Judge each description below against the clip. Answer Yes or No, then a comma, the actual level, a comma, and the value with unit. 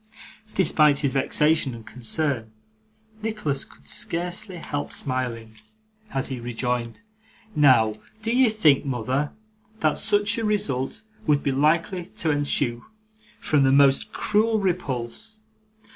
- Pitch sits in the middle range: Yes, medium, 145 Hz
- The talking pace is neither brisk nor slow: No, slow, 120 wpm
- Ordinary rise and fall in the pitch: No, wide, 6.2 semitones